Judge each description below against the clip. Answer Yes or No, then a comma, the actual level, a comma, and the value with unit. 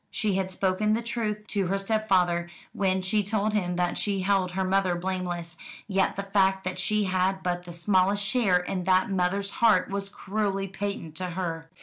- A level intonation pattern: Yes, narrow, 1.8 semitones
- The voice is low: No, high, 190 Hz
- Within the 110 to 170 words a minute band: No, average, 190 wpm